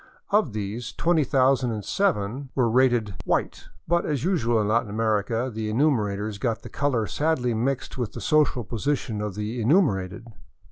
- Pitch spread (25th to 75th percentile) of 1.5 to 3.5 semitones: No, average, 4.4 semitones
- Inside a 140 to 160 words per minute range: Yes, average, 150 wpm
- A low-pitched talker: Yes, low, 120 Hz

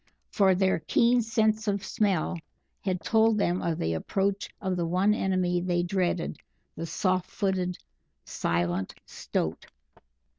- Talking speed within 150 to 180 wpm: No, slow, 135 wpm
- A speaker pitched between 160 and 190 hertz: Yes, medium, 185 Hz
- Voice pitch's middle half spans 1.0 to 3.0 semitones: Yes, average, 2.7 semitones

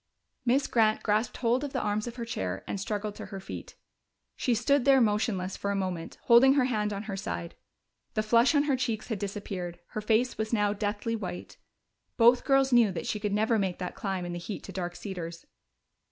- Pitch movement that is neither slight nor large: Yes, average, 3.6 semitones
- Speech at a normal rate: No, fast, 210 wpm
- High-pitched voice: Yes, high, 215 Hz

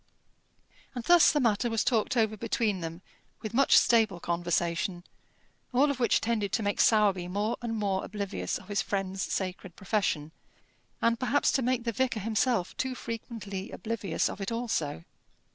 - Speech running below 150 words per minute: No, average, 160 wpm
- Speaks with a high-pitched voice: Yes, high, 215 Hz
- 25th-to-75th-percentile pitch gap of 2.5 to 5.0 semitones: Yes, average, 3.6 semitones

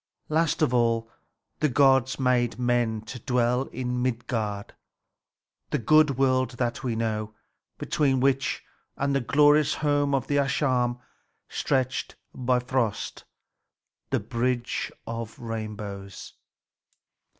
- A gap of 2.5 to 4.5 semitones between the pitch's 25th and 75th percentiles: Yes, average, 2.8 semitones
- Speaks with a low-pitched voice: Yes, low, 125 Hz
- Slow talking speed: Yes, slow, 110 wpm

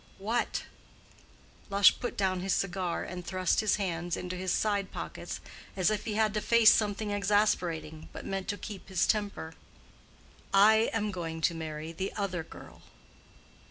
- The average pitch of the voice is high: Yes, high, 195 Hz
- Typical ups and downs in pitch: Yes, average, 3.0 semitones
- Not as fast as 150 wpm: No, average, 160 wpm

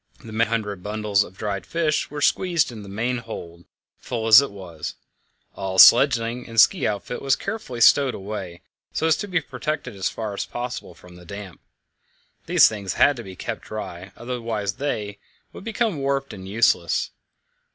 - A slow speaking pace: No, average, 170 wpm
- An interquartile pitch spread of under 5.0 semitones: No, average, 5.3 semitones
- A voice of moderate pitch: No, low, 110 Hz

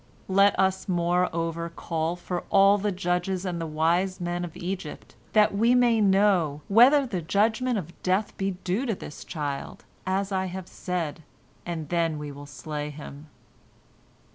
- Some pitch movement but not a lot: Yes, average, 3.2 semitones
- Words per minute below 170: Yes, average, 160 wpm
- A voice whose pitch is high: No, medium, 180 Hz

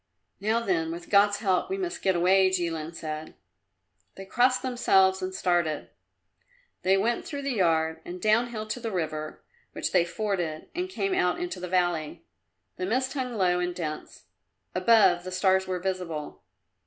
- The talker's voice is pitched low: No, medium, 185 Hz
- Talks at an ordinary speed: Yes, average, 165 wpm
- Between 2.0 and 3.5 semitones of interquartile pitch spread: No, average, 4.0 semitones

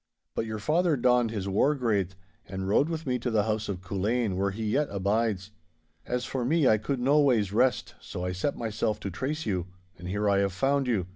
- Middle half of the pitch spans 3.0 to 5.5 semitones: Yes, average, 4.5 semitones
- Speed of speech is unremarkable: No, fast, 215 wpm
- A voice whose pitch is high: No, low, 110 Hz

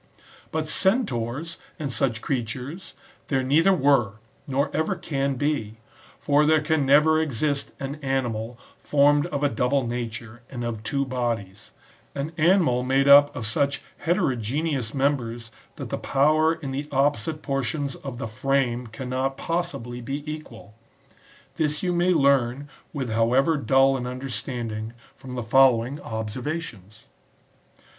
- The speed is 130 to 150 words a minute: Yes, average, 140 wpm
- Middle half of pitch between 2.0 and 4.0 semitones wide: Yes, average, 3.7 semitones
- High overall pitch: No, low, 135 Hz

